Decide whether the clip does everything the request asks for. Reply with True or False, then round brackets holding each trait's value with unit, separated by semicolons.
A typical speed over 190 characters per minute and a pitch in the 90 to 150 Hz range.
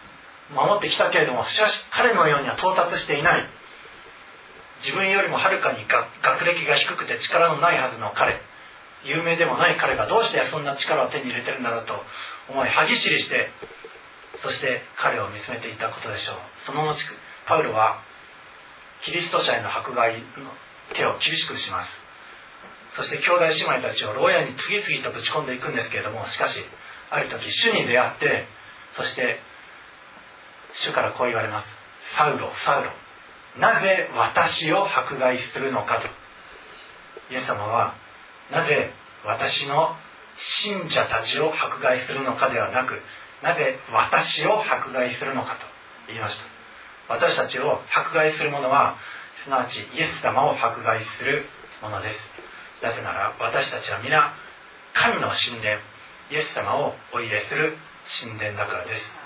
True (300 characters per minute; 140 Hz)